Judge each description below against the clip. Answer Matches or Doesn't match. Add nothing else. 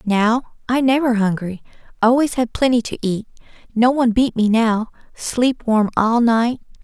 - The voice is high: Matches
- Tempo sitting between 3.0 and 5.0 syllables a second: Matches